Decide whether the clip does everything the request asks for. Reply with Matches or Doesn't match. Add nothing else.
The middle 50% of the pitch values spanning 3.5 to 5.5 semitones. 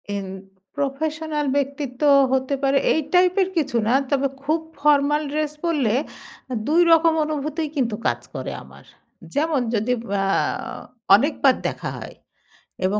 Doesn't match